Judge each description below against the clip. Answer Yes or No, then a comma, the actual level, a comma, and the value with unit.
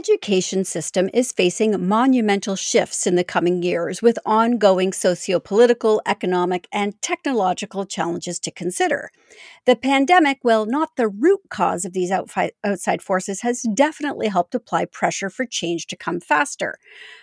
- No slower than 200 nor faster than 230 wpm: No, average, 150 wpm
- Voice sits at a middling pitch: No, high, 200 Hz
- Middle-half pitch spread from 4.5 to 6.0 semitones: Yes, average, 4.8 semitones